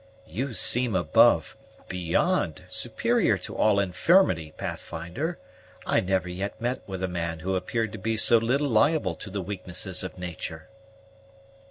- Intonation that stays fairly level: No, average, 4.3 semitones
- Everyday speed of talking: Yes, average, 145 wpm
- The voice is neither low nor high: No, very low, 95 Hz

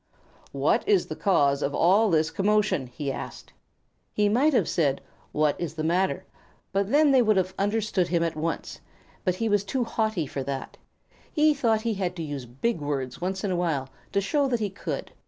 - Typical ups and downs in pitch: No, wide, 5.8 semitones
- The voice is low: No, medium, 185 Hz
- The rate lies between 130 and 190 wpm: No, average, 200 wpm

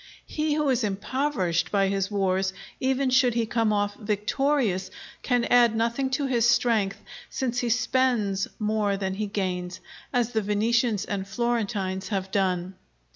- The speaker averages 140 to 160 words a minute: Yes, average, 150 wpm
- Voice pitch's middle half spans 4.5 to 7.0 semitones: No, average, 4.0 semitones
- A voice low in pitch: No, high, 215 Hz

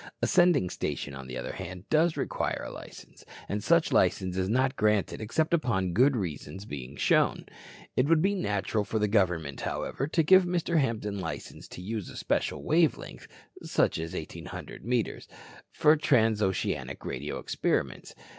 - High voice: No, low, 105 Hz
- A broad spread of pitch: Yes, wide, 8.9 semitones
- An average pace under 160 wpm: No, average, 165 wpm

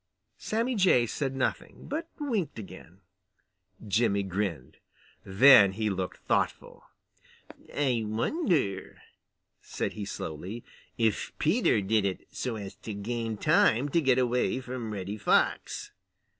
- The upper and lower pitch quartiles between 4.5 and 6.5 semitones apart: Yes, average, 5.0 semitones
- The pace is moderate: No, slow, 120 wpm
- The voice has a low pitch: Yes, low, 115 Hz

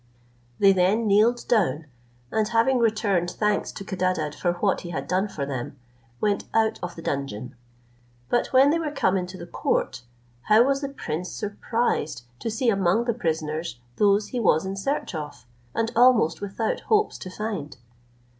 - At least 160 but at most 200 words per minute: Yes, average, 170 wpm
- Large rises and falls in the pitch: No, average, 4.9 semitones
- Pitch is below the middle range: No, high, 200 Hz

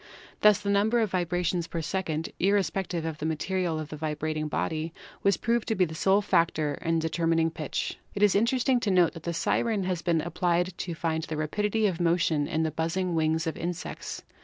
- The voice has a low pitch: No, medium, 170 Hz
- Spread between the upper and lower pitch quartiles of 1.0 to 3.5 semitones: Yes, average, 3.2 semitones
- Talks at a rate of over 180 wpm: Yes, fast, 205 wpm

